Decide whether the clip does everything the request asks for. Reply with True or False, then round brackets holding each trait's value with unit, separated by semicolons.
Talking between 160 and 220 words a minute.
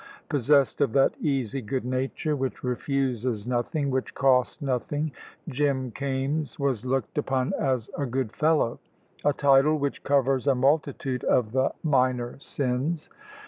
False (140 wpm)